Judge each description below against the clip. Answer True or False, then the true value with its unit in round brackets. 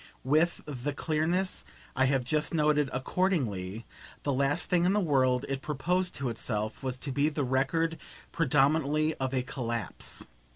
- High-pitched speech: False (140 Hz)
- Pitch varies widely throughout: False (3.6 semitones)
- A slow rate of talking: False (155 wpm)